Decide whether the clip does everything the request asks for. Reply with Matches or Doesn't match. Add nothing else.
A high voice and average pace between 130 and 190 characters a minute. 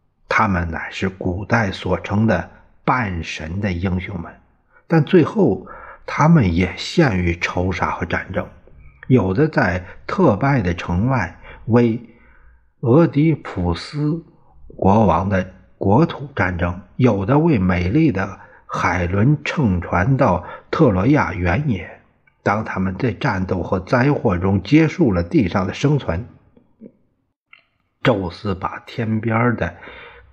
Doesn't match